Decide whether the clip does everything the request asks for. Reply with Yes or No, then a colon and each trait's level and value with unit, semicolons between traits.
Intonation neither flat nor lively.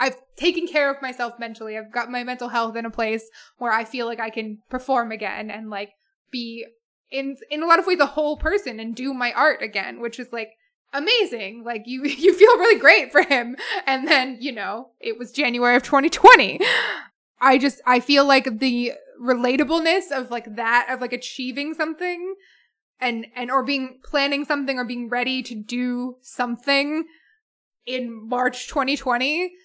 Yes: average, 3.3 semitones